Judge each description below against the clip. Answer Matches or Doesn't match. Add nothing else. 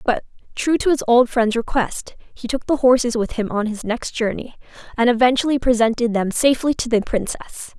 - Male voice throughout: Doesn't match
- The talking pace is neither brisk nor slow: Matches